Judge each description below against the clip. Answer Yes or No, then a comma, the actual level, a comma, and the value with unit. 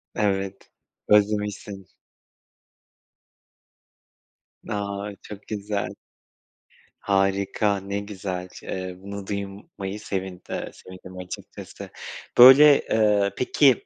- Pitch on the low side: Yes, low, 100 Hz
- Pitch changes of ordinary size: No, narrow, 1.3 semitones